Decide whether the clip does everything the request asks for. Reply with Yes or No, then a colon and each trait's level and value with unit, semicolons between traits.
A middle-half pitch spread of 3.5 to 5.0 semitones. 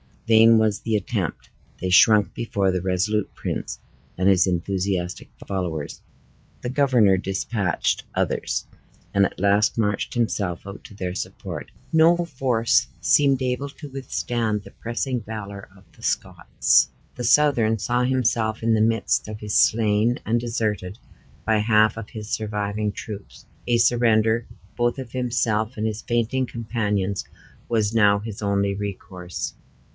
No: average, 2.9 semitones